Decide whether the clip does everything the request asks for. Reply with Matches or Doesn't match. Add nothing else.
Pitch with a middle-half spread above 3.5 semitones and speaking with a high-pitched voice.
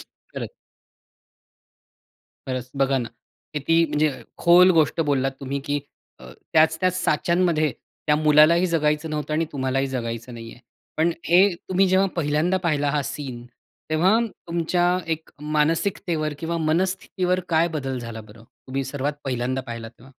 Doesn't match